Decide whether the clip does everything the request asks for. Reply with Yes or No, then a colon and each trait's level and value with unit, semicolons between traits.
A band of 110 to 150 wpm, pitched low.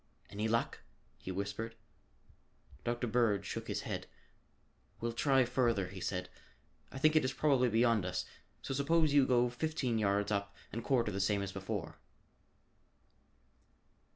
Yes: average, 145 wpm; low, 115 Hz